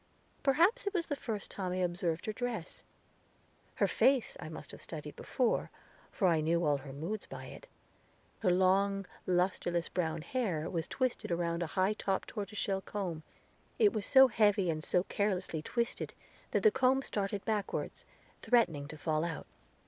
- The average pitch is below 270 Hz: Yes, high, 190 Hz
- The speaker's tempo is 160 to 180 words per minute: Yes, average, 170 wpm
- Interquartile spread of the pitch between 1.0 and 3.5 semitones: No, average, 5.1 semitones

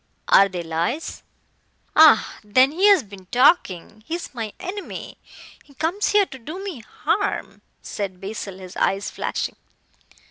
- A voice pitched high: Yes, high, 230 Hz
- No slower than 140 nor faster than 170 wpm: Yes, average, 145 wpm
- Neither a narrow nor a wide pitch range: No, wide, 8.9 semitones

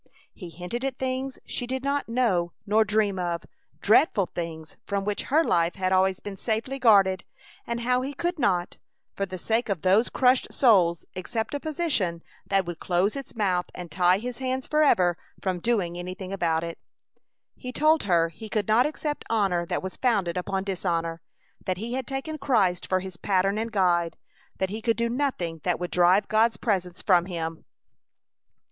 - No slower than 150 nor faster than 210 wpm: Yes, average, 180 wpm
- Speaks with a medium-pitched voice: No, high, 195 Hz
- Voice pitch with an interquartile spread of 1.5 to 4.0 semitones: No, average, 5.3 semitones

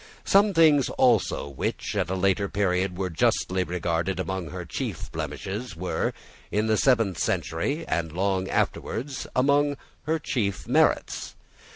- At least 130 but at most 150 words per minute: Yes, average, 145 wpm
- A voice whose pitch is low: Yes, low, 100 Hz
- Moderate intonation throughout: No, wide, 6.2 semitones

